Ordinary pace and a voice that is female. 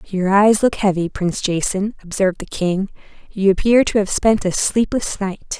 Yes: average, 180 wpm; female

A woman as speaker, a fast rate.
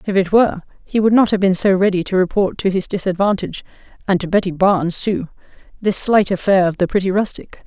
Yes: female; fast, 210 wpm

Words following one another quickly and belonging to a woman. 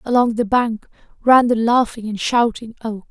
No: average, 175 wpm; female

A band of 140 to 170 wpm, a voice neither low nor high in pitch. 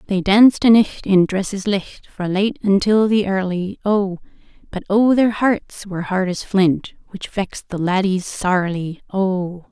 No: average, 165 wpm; high, 195 Hz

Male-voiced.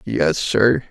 Yes: male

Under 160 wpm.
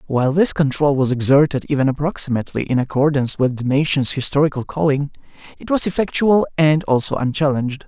Yes: average, 150 wpm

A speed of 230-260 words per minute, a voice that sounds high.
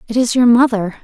Yes: fast, 235 wpm; high, 235 Hz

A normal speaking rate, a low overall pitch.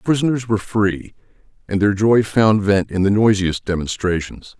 Yes: average, 170 wpm; low, 105 Hz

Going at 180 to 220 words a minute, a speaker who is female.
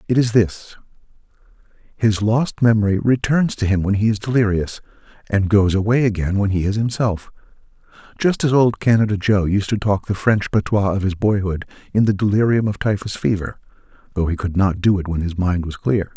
No: average, 195 wpm; male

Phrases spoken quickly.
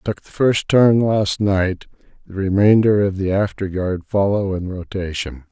No: average, 165 wpm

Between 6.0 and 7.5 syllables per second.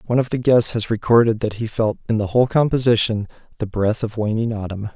Yes: 6.2 syllables/s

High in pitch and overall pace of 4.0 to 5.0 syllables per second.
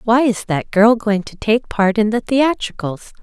Yes: high, 220 Hz; 4.3 syllables/s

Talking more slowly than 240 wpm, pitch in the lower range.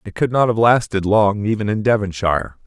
Yes: fast, 205 wpm; low, 105 Hz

